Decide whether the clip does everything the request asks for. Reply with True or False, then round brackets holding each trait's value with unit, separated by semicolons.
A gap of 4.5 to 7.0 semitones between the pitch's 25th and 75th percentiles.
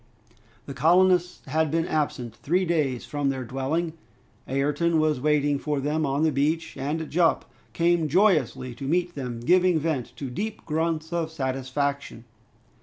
False (3.4 semitones)